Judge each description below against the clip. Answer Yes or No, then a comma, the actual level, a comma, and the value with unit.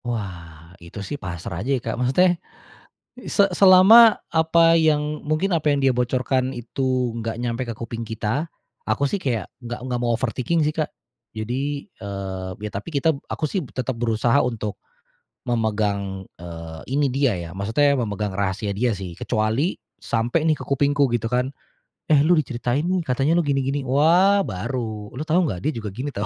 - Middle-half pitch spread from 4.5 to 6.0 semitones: Yes, wide, 5.4 semitones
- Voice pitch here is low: Yes, low, 125 Hz